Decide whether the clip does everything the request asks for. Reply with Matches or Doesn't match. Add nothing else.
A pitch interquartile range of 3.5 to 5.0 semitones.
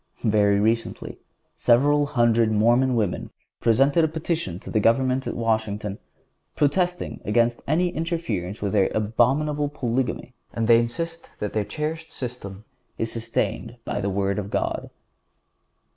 Doesn't match